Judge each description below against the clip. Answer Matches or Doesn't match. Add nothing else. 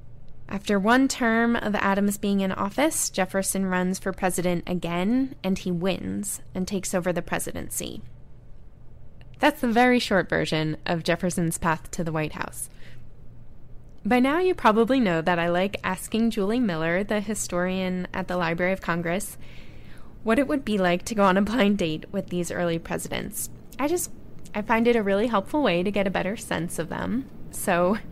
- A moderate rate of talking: Matches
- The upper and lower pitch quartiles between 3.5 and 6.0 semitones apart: Matches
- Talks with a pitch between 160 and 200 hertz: Matches